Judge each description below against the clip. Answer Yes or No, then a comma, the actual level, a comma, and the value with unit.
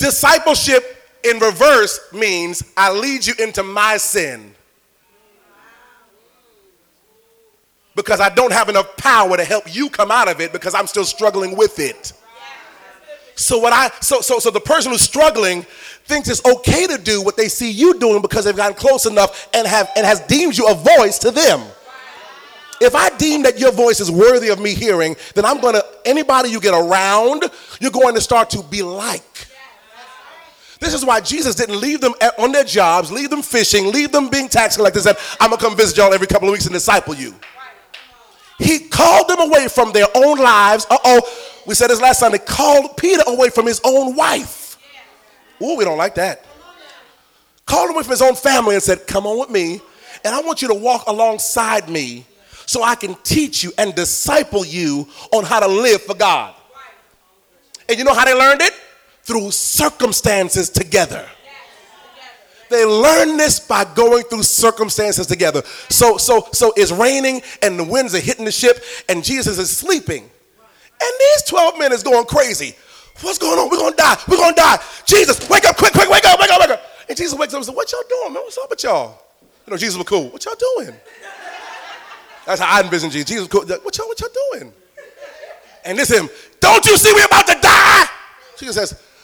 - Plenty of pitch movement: Yes, wide, 6.2 semitones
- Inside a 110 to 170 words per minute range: No, average, 200 wpm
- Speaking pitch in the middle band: No, high, 240 Hz